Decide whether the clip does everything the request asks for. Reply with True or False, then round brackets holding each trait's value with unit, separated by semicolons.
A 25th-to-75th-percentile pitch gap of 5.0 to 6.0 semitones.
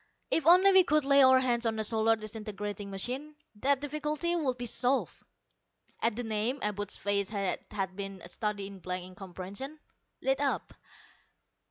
True (5.5 semitones)